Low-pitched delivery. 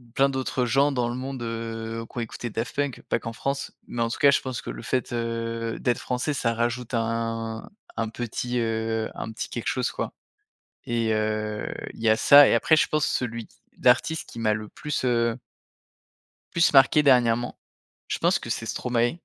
Yes: low, 115 Hz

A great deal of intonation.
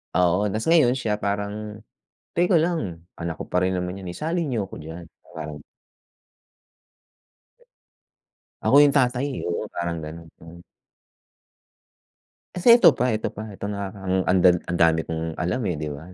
Yes: wide, 6.3 semitones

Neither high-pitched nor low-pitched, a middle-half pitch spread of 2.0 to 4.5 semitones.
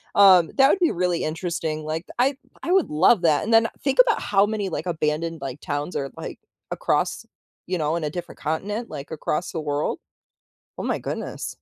No: medium, 170 Hz; average, 5.2 semitones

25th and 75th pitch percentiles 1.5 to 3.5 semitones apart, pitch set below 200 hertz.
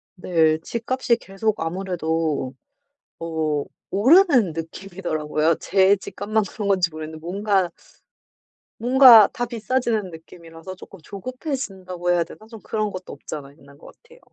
No: average, 5.1 semitones; high, 190 Hz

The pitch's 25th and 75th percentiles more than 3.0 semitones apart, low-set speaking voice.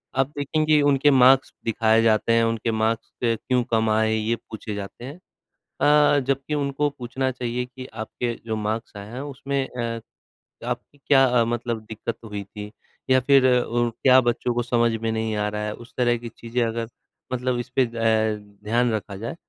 No: average, 2.7 semitones; low, 120 Hz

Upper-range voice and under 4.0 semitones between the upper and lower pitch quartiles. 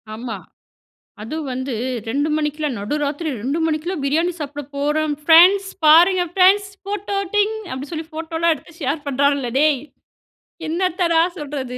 Yes: very high, 310 Hz; average, 3.4 semitones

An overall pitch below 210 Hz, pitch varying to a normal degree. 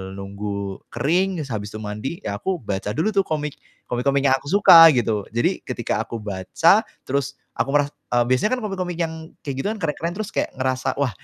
No: low, 135 Hz; wide, 7.5 semitones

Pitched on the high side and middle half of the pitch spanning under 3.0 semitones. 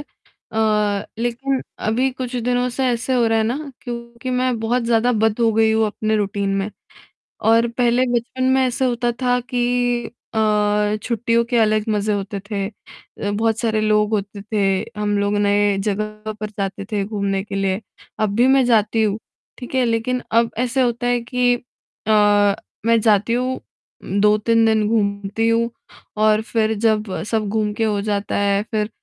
Yes: high, 220 Hz; narrow, 2.4 semitones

